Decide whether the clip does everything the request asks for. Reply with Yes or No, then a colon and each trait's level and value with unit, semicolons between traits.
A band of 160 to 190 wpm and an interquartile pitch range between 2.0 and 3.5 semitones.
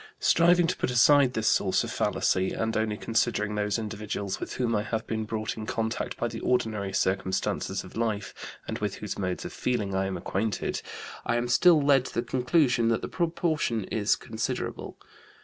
Yes: average, 185 wpm; average, 3.0 semitones